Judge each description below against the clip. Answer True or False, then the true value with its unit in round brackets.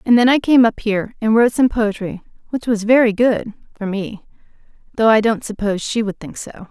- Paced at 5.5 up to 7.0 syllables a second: True (5.9 syllables/s)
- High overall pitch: True (220 Hz)